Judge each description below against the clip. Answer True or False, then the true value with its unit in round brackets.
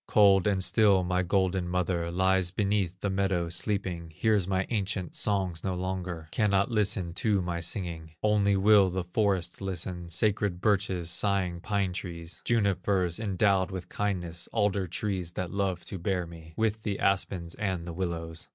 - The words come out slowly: False (160 wpm)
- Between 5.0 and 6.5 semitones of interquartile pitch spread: False (2.4 semitones)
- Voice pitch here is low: True (95 Hz)